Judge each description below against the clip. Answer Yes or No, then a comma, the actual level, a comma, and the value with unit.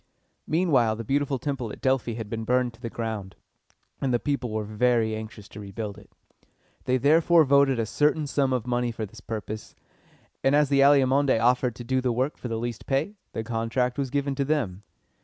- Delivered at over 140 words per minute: Yes, average, 200 wpm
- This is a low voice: Yes, low, 125 Hz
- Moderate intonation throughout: Yes, average, 3.7 semitones